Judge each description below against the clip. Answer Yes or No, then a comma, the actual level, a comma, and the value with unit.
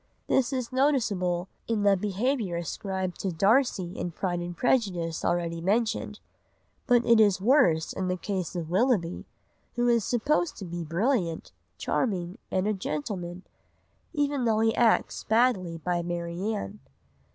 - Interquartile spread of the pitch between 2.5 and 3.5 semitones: No, average, 5.1 semitones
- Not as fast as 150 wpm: Yes, average, 140 wpm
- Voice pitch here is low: No, high, 195 Hz